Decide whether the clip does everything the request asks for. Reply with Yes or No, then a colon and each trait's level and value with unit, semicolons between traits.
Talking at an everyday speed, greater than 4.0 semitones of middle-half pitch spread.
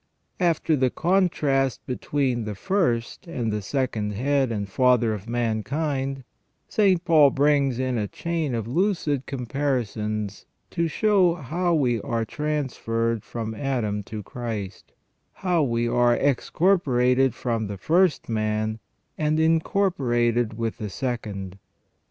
No: slow, 130 wpm; average, 5.1 semitones